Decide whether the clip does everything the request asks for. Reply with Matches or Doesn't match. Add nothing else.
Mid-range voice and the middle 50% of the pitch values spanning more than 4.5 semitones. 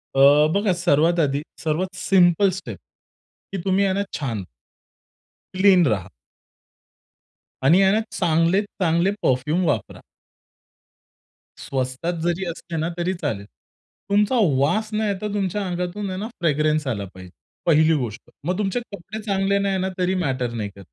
Matches